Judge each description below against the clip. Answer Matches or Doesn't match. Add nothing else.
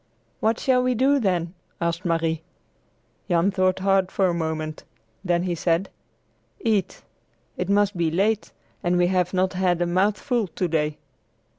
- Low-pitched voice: Doesn't match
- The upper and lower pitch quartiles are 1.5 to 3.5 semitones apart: Matches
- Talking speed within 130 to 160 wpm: Matches